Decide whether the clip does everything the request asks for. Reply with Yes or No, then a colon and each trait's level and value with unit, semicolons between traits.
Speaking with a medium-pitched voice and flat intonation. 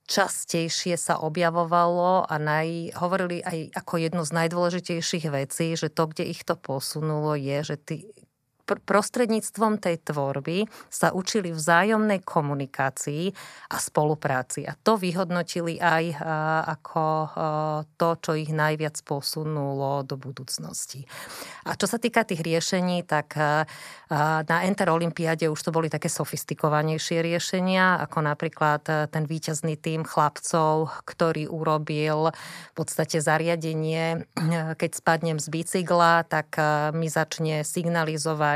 Yes: medium, 160 Hz; narrow, 2.0 semitones